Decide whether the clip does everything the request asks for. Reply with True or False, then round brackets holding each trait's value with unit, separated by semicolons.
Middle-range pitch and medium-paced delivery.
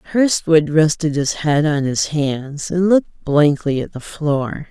True (150 Hz; 165 wpm)